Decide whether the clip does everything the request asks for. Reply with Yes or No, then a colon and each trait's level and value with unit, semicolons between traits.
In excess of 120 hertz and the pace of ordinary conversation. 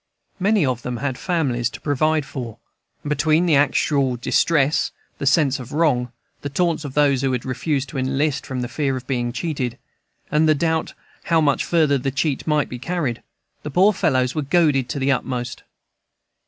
Yes: medium, 140 Hz; average, 185 wpm